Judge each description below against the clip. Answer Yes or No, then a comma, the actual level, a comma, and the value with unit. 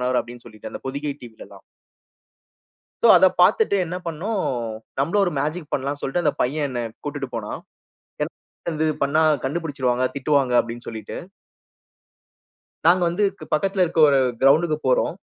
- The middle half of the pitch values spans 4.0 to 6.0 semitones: Yes, average, 4.5 semitones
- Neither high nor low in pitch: Yes, medium, 145 Hz